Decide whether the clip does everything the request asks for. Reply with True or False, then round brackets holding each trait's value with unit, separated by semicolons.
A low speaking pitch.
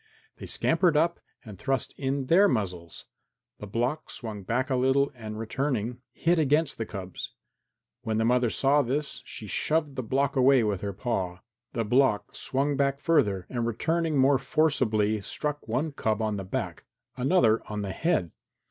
True (125 Hz)